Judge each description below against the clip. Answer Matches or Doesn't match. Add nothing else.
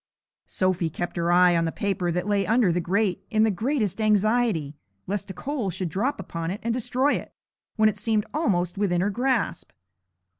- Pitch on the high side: Matches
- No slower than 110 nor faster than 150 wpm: Doesn't match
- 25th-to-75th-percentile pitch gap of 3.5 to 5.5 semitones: Matches